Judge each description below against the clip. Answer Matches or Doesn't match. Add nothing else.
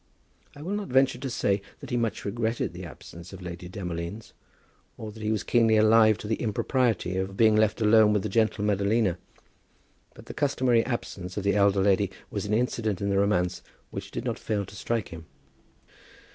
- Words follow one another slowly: Doesn't match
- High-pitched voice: Doesn't match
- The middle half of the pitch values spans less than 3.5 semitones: Matches